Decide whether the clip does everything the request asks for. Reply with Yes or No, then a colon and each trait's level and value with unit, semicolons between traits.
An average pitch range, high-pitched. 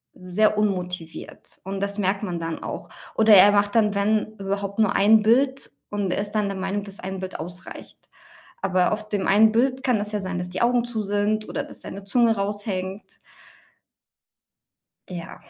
No: narrow, 2.1 semitones; high, 205 Hz